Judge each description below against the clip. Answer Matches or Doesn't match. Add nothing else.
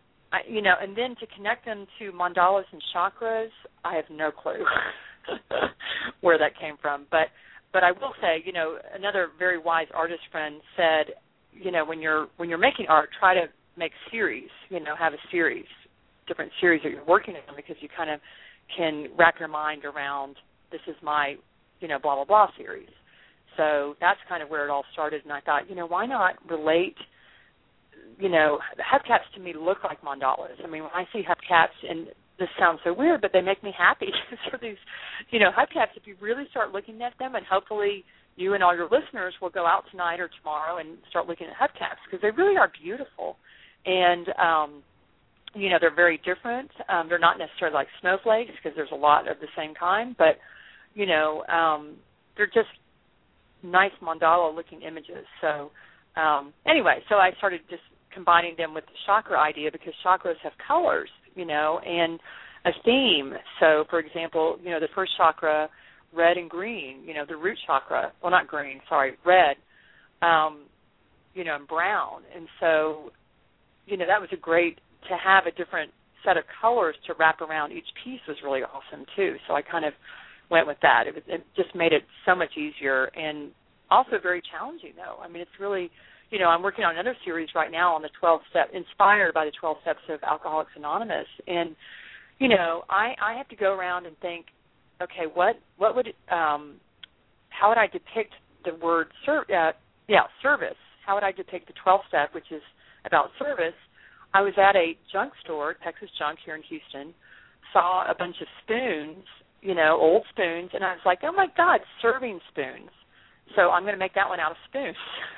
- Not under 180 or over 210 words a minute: Matches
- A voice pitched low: Doesn't match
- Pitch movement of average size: Matches